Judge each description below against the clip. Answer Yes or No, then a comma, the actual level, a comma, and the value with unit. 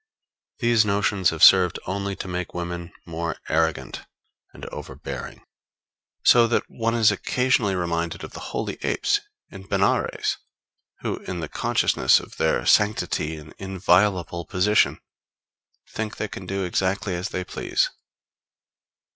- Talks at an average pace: No, slow, 130 wpm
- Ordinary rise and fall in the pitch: Yes, average, 3.3 semitones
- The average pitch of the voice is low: Yes, very low, 95 Hz